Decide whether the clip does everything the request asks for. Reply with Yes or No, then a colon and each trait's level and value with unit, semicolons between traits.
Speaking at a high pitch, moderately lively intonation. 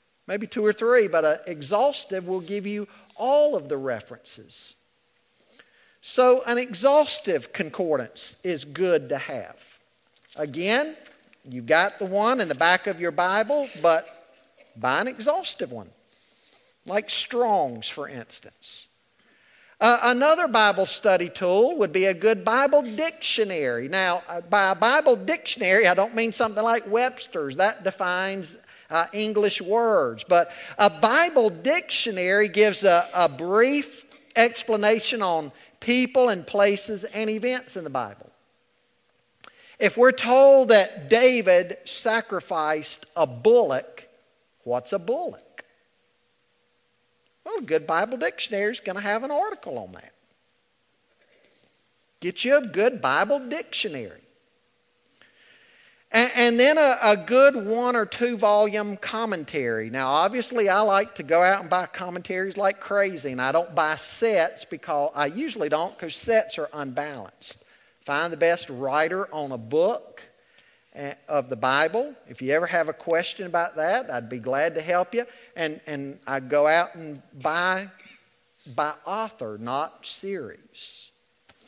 No: high, 205 Hz; wide, 6.1 semitones